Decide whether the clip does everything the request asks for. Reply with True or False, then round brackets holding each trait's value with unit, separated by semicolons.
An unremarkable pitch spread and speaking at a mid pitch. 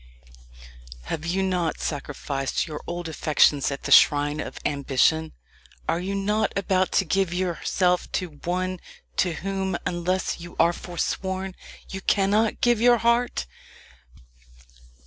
True (3.2 semitones; 180 Hz)